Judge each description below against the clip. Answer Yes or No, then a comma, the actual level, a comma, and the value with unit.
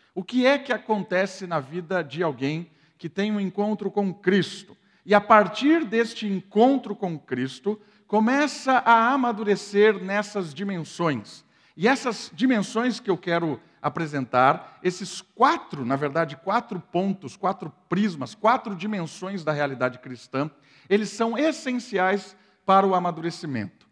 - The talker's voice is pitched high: Yes, high, 195 Hz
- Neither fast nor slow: Yes, average, 135 wpm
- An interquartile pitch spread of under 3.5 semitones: No, average, 4.4 semitones